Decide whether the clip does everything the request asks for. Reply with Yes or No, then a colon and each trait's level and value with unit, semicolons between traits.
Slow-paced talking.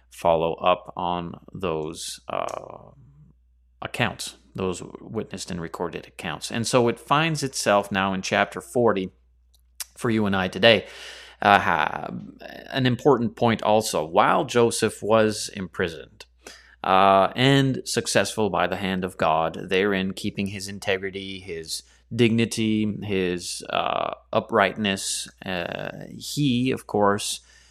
Yes: slow, 120 wpm